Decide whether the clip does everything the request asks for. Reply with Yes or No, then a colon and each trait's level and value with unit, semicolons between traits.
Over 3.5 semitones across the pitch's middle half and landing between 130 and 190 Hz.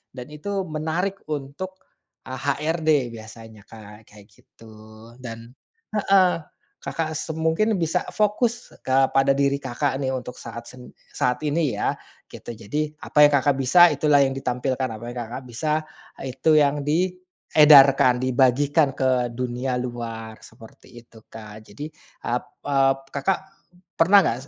Yes: average, 4.2 semitones; low, 135 Hz